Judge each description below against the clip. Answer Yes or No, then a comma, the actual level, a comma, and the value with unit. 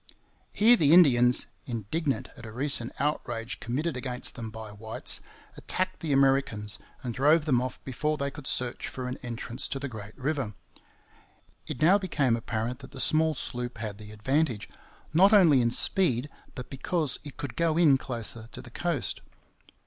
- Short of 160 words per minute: No, average, 170 wpm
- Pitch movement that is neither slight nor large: Yes, average, 4.4 semitones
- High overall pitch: No, low, 130 Hz